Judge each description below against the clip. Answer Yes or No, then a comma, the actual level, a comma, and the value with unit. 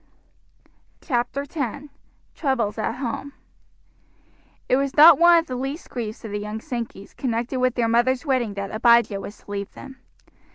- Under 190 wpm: Yes, average, 160 wpm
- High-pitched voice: Yes, high, 245 Hz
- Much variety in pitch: No, average, 3.7 semitones